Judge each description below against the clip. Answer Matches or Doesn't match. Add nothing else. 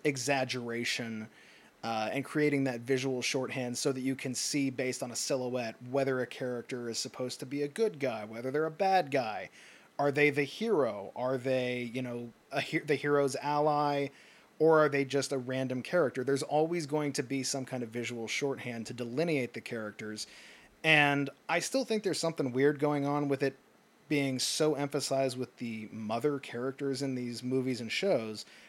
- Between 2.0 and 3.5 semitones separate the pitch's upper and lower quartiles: Matches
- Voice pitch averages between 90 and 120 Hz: Doesn't match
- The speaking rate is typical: Matches